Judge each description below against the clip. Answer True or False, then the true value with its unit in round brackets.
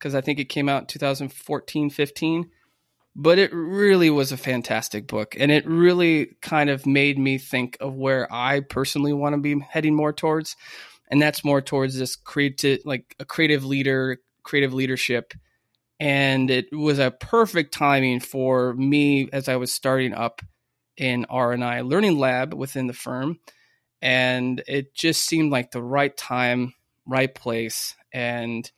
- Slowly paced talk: False (160 wpm)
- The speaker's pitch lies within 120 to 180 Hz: True (135 Hz)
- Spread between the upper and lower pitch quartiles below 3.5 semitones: True (2.6 semitones)